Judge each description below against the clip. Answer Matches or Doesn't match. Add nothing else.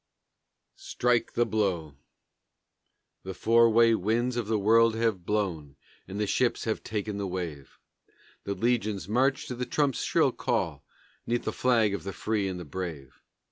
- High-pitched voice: Doesn't match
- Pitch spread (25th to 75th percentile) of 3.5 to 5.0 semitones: Matches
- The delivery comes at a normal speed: Matches